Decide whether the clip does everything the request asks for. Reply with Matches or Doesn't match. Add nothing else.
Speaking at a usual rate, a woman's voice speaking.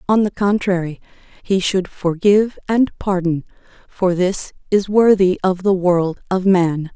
Matches